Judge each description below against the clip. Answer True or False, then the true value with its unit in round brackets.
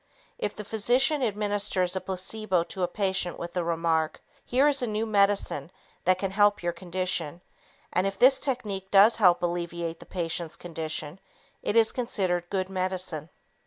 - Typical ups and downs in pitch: True (3.3 semitones)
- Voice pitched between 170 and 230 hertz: True (185 Hz)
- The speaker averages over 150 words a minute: True (165 wpm)